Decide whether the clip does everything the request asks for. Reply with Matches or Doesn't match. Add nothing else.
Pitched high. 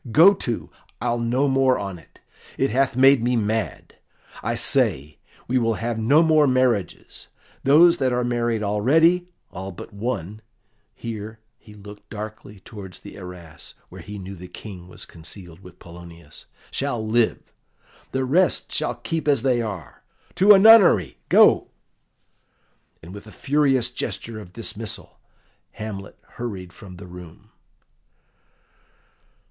Doesn't match